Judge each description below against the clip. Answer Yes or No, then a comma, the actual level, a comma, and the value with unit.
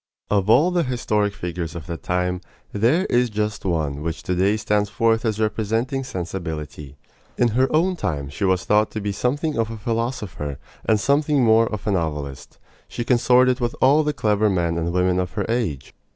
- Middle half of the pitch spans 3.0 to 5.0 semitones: No, wide, 5.5 semitones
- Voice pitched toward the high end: No, low, 105 Hz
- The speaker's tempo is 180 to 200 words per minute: Yes, average, 190 wpm